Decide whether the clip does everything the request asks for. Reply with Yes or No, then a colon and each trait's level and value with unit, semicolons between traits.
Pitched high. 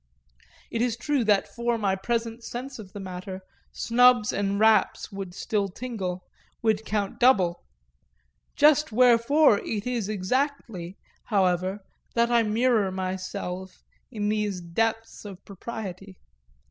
Yes: high, 210 Hz